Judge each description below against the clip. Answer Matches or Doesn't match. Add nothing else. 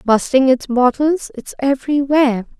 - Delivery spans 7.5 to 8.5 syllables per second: Doesn't match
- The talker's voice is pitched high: Matches